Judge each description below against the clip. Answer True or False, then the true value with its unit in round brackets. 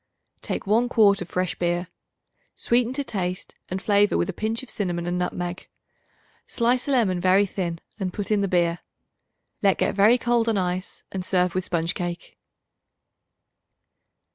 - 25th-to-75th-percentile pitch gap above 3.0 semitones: True (3.4 semitones)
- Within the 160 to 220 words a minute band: True (165 wpm)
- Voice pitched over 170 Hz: True (190 Hz)